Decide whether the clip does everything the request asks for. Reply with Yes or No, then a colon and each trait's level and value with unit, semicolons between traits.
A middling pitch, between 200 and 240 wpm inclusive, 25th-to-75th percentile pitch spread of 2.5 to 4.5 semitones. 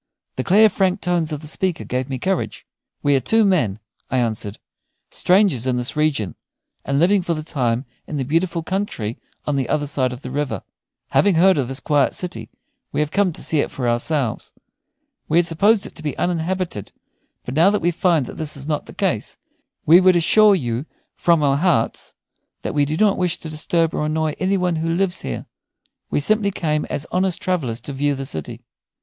No: medium, 155 Hz; fast, 205 wpm; average, 5.1 semitones